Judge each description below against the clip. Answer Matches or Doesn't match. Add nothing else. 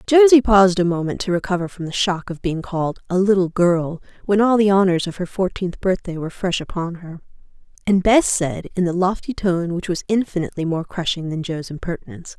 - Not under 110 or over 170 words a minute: Doesn't match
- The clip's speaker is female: Matches